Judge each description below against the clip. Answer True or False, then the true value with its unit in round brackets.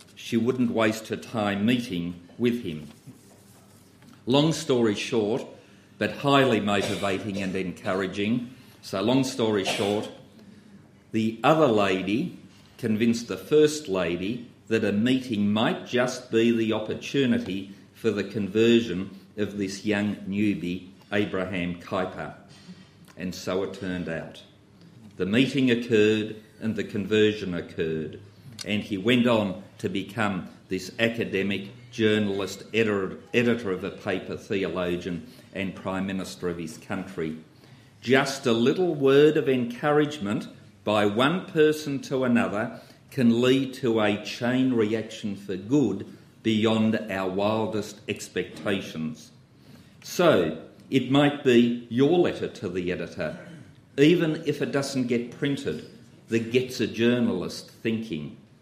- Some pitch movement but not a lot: True (4.2 semitones)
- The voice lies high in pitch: False (110 Hz)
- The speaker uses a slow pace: True (125 wpm)